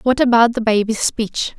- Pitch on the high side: Yes, high, 230 Hz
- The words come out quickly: No, average, 190 wpm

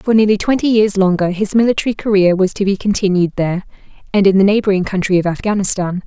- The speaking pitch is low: No, high, 195 Hz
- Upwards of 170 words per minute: Yes, average, 200 wpm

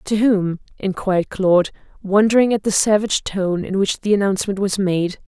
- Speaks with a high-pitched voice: Yes, high, 195 Hz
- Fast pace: No, average, 170 wpm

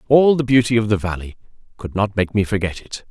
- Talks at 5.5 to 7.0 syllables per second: Yes, 5.9 syllables/s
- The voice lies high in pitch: No, low, 110 Hz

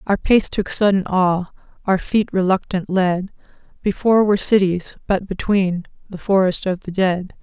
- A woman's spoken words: Yes, female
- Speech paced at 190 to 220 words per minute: No, average, 155 wpm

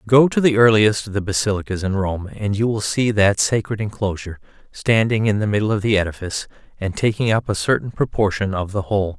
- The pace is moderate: No, fast, 210 wpm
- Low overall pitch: Yes, low, 105 Hz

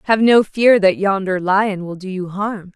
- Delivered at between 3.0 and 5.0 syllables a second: Yes, 4.3 syllables/s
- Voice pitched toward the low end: No, high, 200 Hz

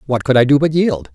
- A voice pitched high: No, low, 135 Hz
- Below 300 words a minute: No, fast, 315 wpm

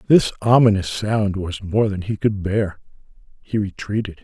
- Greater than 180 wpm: No, average, 155 wpm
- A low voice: Yes, low, 100 Hz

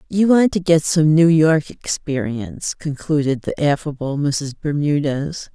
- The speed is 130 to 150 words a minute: Yes, average, 140 wpm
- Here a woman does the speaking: Yes, female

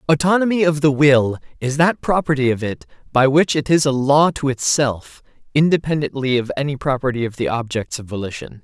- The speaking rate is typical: Yes, average, 180 wpm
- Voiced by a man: Yes, male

